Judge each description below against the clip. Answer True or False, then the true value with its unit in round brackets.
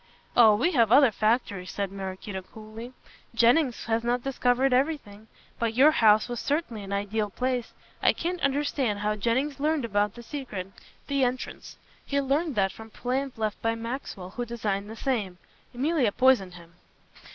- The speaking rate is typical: True (165 wpm)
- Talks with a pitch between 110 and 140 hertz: False (235 Hz)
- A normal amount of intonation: True (4.4 semitones)